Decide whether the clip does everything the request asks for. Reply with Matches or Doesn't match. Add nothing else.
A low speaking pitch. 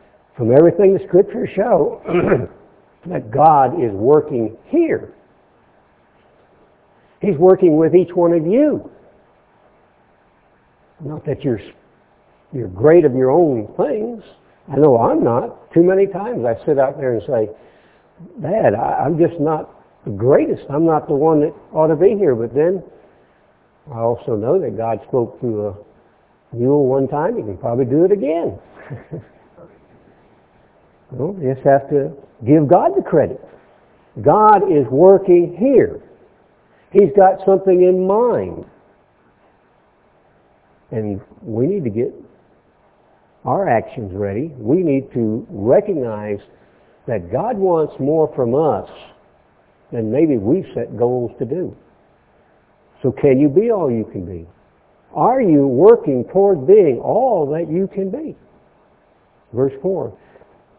Doesn't match